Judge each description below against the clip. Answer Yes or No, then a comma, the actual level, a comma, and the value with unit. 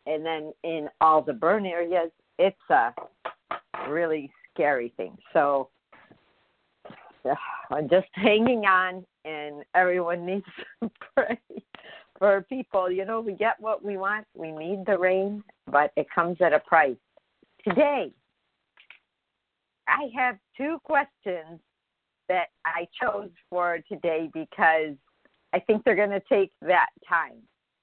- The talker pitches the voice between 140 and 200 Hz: Yes, medium, 185 Hz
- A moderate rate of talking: No, slow, 130 wpm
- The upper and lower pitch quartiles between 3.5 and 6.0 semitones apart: Yes, average, 4.6 semitones